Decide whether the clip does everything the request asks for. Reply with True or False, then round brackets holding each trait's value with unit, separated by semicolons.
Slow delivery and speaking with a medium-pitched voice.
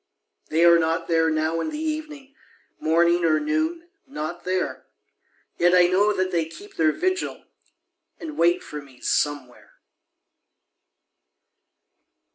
True (125 wpm; 175 Hz)